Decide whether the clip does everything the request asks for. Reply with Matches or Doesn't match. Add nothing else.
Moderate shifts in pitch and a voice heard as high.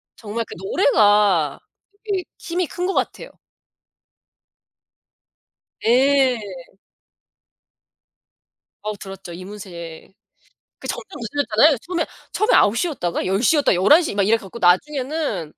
Doesn't match